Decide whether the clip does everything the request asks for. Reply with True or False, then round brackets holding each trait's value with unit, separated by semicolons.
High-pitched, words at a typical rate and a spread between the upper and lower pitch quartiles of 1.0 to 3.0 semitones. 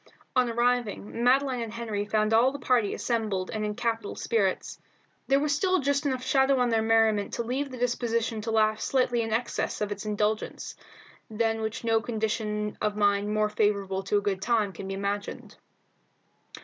True (225 Hz; 180 wpm; 2.7 semitones)